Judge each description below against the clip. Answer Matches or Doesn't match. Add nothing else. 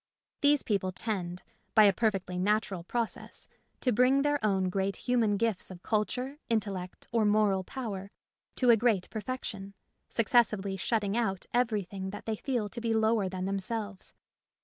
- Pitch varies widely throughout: Doesn't match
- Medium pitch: Doesn't match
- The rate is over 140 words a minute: Matches